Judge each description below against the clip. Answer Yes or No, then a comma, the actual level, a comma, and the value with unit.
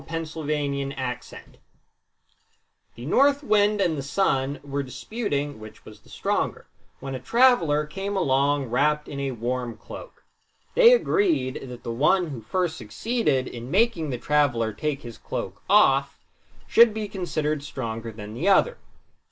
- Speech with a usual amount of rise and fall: No, wide, 7.0 semitones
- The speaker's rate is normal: Yes, average, 145 wpm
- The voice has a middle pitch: Yes, medium, 145 Hz